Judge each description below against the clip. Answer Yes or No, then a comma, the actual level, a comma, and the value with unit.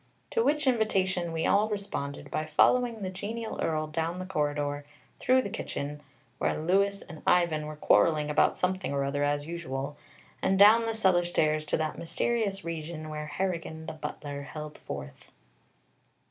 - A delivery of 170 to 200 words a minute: No, average, 160 wpm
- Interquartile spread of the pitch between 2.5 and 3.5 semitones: No, average, 4.6 semitones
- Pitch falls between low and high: Yes, medium, 165 Hz